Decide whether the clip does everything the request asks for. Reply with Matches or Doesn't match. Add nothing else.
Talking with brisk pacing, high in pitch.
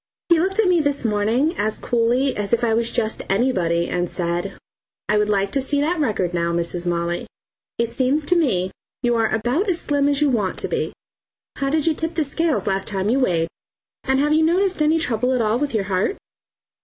Matches